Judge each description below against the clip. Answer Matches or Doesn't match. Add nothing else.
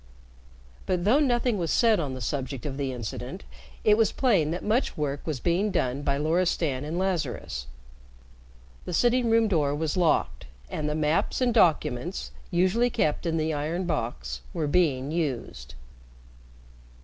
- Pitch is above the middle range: Doesn't match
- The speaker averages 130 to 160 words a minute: Matches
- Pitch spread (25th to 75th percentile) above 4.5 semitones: Matches